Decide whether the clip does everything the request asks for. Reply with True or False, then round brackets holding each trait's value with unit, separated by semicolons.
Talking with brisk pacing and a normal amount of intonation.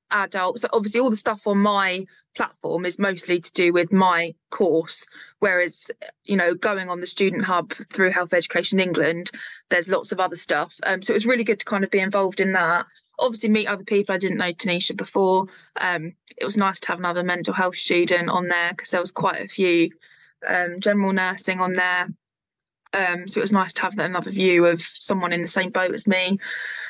False (210 wpm; 2.2 semitones)